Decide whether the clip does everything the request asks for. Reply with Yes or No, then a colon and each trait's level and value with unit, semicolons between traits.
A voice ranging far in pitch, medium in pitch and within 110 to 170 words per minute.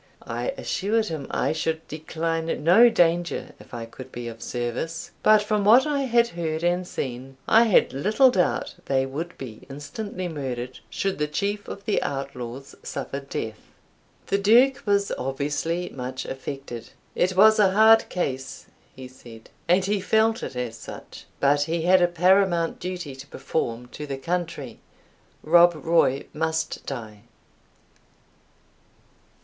Yes: wide, 6.5 semitones; medium, 165 Hz; average, 150 wpm